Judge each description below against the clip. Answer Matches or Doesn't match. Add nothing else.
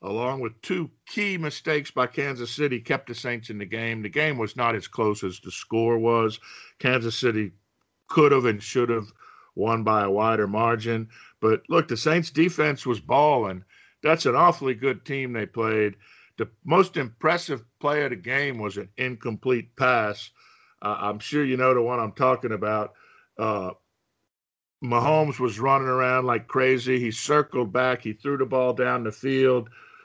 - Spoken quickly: Doesn't match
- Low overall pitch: Matches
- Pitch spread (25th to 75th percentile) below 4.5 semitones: Matches